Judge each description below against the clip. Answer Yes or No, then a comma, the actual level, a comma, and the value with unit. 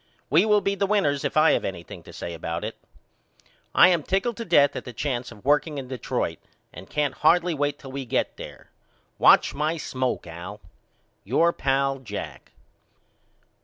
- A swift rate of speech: No, average, 180 wpm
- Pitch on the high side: No, medium, 140 Hz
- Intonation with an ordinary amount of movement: Yes, average, 5.0 semitones